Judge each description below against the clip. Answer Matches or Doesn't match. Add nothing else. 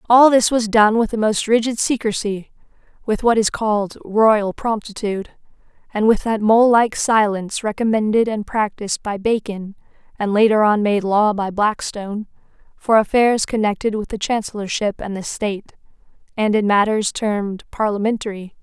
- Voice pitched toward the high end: Matches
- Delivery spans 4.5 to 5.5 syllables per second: Matches